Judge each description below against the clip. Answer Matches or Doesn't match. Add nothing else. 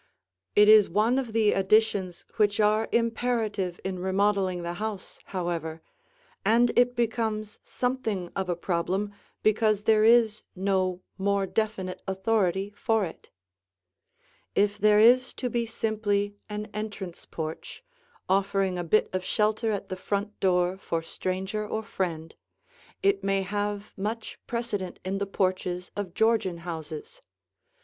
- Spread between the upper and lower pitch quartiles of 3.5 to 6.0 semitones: Doesn't match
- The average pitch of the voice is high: Matches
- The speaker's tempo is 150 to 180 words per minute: Doesn't match